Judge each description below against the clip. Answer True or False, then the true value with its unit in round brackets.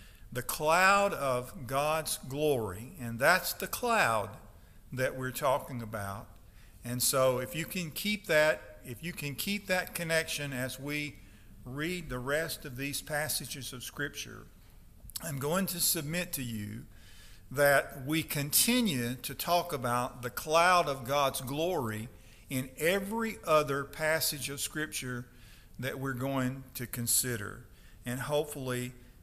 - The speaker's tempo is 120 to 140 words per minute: True (135 wpm)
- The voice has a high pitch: False (135 Hz)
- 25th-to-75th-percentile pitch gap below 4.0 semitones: False (4.3 semitones)